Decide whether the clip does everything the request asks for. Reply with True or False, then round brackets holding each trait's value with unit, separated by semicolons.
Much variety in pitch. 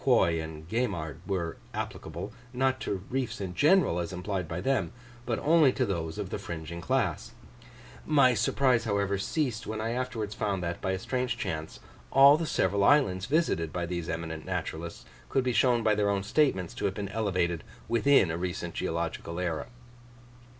True (6.7 semitones)